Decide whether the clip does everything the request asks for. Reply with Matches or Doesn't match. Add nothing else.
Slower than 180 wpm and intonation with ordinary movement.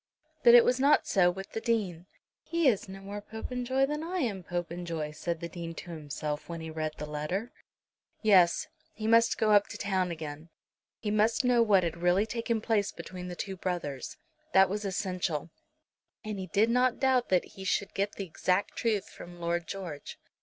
Doesn't match